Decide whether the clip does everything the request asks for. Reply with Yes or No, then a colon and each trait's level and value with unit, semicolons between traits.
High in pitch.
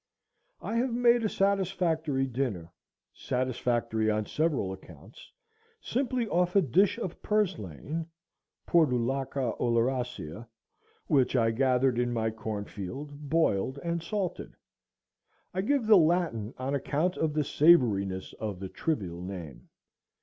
No: low, 135 Hz